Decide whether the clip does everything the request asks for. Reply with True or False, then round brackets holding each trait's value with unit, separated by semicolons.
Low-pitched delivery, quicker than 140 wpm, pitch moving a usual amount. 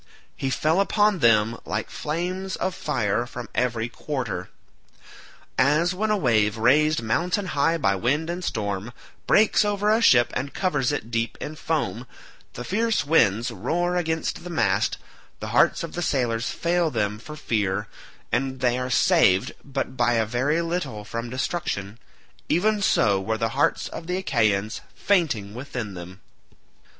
False (130 Hz; 155 wpm; 7.1 semitones)